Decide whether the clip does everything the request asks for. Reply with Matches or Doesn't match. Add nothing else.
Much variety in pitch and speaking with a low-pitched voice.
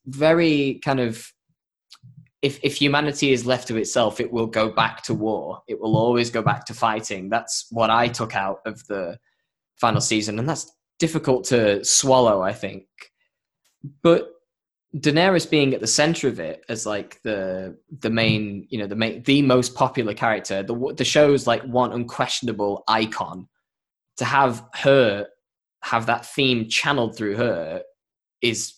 Doesn't match